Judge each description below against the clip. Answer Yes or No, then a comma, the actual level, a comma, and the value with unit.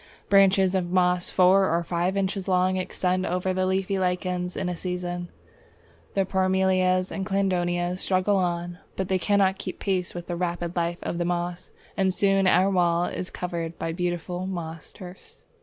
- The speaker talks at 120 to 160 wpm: No, average, 170 wpm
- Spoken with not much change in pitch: Yes, narrow, 1.3 semitones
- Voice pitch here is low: No, medium, 180 Hz